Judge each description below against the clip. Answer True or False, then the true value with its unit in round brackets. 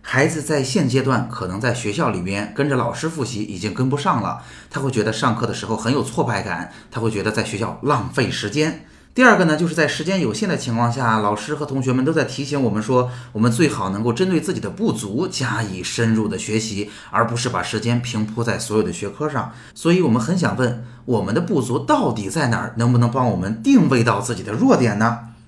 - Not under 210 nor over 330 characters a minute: False (340 characters per minute)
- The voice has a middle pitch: False (120 Hz)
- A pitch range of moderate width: True (4.5 semitones)